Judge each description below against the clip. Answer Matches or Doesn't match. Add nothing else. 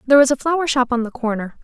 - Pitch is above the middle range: Matches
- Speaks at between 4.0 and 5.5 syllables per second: Doesn't match